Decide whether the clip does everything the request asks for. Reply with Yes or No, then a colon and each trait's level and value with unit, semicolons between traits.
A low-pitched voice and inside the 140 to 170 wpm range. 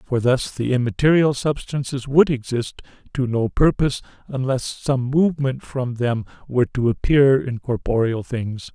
Yes: low, 130 Hz; average, 145 wpm